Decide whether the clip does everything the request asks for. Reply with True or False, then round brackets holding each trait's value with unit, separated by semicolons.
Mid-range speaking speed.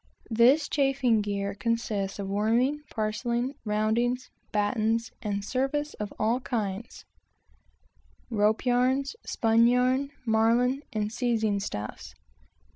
False (110 wpm)